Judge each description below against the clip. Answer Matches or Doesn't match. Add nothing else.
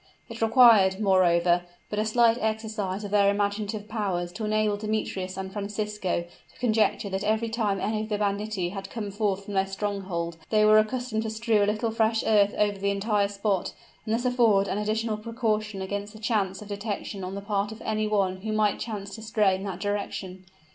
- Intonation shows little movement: Matches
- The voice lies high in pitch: Matches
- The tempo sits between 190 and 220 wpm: Matches